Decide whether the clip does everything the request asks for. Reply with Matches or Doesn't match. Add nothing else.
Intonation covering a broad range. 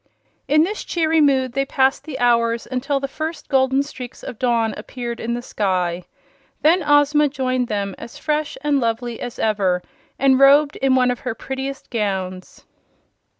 Doesn't match